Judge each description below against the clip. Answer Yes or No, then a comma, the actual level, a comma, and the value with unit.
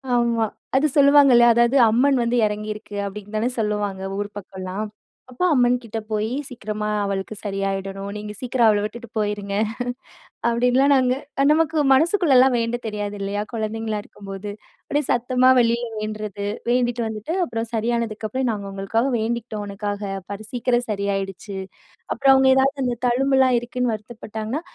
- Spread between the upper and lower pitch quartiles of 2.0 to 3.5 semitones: Yes, average, 3.2 semitones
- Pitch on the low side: No, high, 225 Hz